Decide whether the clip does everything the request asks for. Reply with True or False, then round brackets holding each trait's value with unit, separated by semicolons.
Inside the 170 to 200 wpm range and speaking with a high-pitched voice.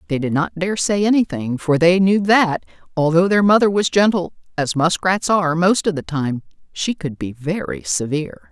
False (190 wpm; 170 Hz)